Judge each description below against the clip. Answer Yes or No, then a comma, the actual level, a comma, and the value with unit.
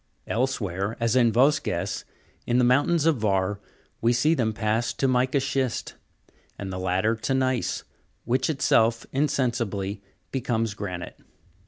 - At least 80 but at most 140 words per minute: Yes, slow, 135 wpm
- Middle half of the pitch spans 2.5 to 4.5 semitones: Yes, average, 3.9 semitones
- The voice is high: No, low, 115 Hz